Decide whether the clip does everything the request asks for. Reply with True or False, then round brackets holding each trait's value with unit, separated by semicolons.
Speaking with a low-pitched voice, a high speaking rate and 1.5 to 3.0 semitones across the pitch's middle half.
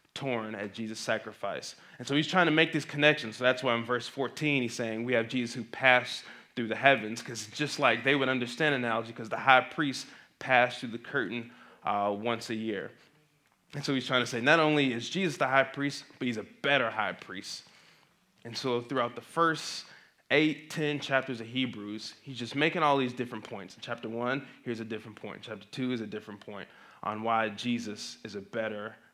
False (125 Hz; 210 wpm; 3.8 semitones)